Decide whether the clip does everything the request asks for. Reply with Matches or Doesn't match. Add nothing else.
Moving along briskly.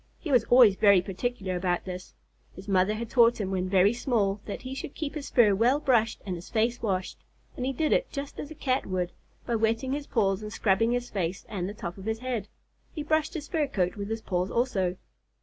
Matches